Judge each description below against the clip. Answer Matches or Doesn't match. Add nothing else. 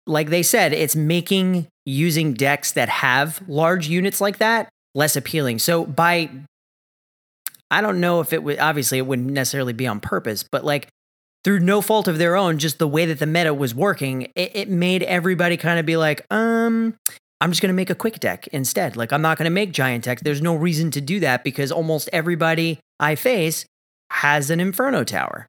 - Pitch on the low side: Doesn't match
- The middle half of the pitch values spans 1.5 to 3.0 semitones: Doesn't match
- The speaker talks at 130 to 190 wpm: Doesn't match